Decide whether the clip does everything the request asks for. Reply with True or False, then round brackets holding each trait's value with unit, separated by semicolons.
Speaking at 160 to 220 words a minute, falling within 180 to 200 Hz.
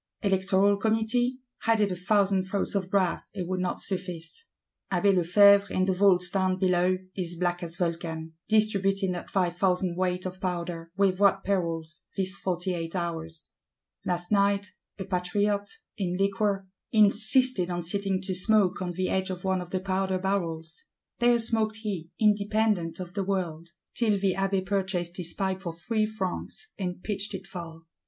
True (165 wpm; 190 Hz)